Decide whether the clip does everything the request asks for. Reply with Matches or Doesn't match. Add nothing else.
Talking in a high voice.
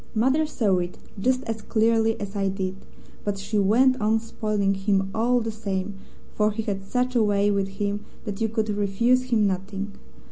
Matches